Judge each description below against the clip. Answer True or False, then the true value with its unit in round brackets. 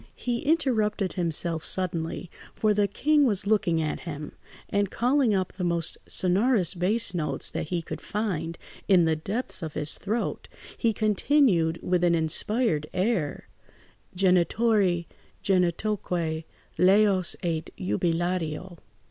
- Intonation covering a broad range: False (4.3 semitones)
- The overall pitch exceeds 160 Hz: True (185 Hz)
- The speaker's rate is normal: False (125 wpm)